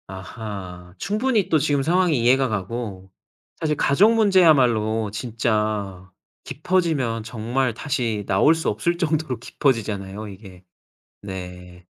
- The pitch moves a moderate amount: No, wide, 7.1 semitones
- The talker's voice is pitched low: Yes, low, 115 Hz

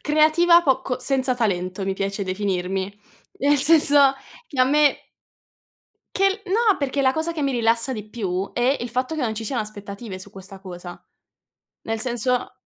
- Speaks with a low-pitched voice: No, high, 245 Hz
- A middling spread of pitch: No, wide, 6.0 semitones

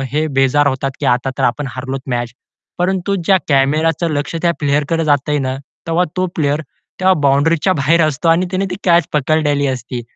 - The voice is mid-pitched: Yes, medium, 150 Hz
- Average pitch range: Yes, average, 3.6 semitones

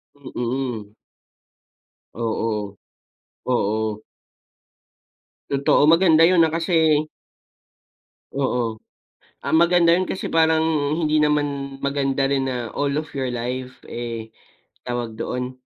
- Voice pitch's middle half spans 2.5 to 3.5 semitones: No, average, 4.6 semitones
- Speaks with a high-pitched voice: No, low, 135 Hz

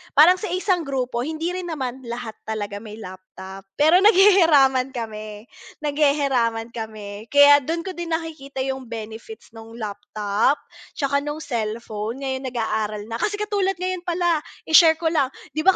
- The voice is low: No, very high, 270 Hz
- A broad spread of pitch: Yes, wide, 6.7 semitones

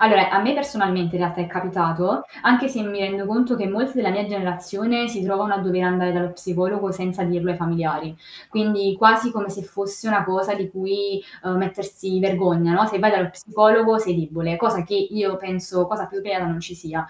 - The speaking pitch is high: Yes, high, 195 Hz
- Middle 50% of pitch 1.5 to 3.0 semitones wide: Yes, narrow, 2.4 semitones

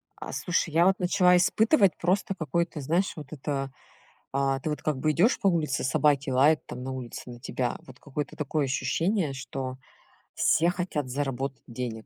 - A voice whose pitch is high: No, medium, 150 Hz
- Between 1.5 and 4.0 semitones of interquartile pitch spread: No, average, 4.6 semitones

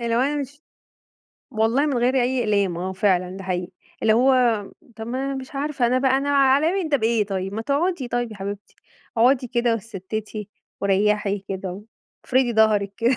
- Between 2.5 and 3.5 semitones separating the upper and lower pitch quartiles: No, average, 4.7 semitones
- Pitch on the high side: Yes, high, 230 Hz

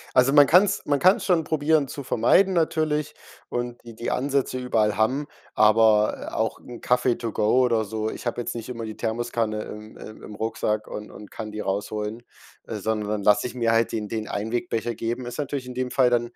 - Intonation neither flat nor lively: Yes, average, 3.3 semitones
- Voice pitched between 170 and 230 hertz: No, low, 120 Hz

